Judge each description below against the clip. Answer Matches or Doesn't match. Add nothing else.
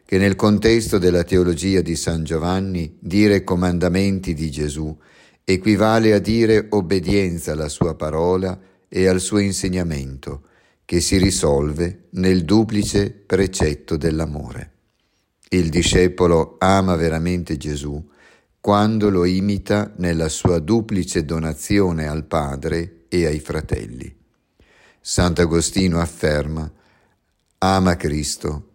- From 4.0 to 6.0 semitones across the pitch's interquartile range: Doesn't match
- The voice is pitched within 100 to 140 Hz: Doesn't match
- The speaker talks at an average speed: Doesn't match